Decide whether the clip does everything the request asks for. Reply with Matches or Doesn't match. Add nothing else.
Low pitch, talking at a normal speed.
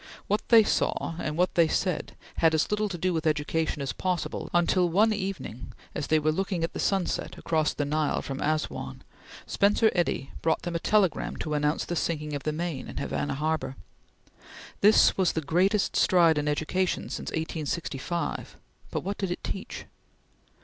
Doesn't match